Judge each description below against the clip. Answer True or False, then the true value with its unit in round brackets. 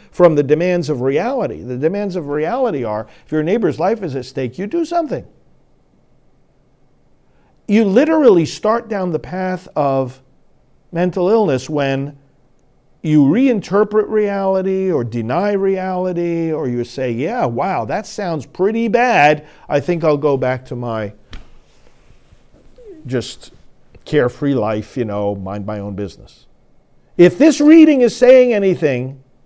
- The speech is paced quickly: False (135 wpm)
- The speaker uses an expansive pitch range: True (7.4 semitones)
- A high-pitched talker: False (160 Hz)